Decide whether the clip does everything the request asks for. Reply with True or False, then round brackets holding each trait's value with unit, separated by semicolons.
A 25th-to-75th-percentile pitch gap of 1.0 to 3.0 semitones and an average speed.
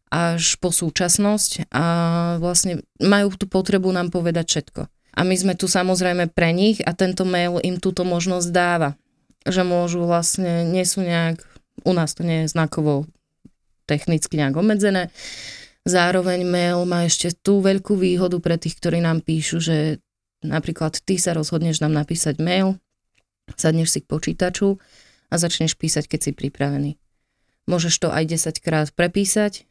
True (2.5 semitones; 155 wpm)